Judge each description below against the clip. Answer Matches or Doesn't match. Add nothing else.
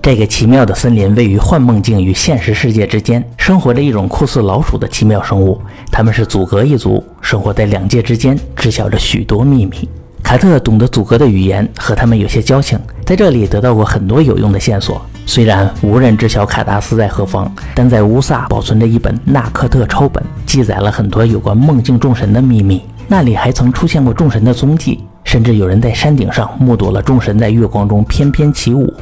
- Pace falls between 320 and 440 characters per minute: Matches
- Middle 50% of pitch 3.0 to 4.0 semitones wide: Matches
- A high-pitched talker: Doesn't match